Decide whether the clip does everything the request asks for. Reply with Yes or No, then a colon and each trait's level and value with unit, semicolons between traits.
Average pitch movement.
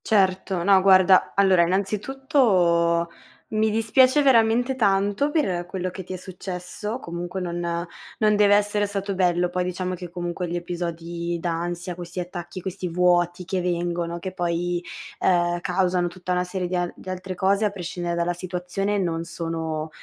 No: narrow, 2.2 semitones